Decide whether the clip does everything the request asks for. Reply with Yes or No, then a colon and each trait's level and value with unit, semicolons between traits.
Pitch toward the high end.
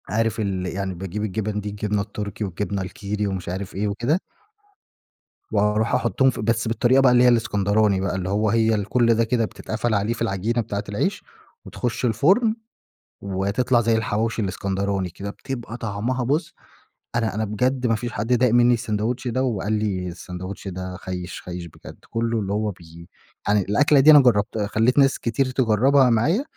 No: low, 110 Hz